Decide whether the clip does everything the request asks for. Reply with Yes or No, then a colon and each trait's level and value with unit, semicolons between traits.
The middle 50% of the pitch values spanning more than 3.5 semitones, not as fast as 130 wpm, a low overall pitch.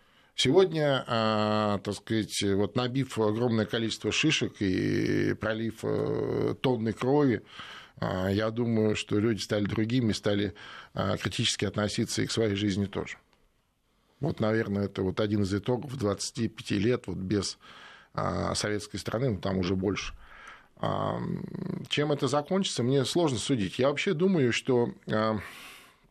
Yes: average, 3.9 semitones; average, 120 wpm; low, 110 Hz